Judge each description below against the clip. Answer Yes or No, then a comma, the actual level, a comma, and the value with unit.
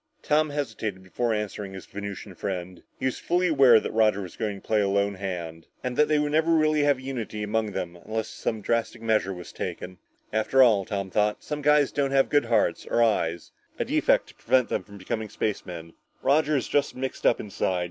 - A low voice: Yes, low, 110 Hz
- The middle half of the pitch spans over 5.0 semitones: Yes, wide, 5.5 semitones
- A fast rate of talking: Yes, fast, 210 wpm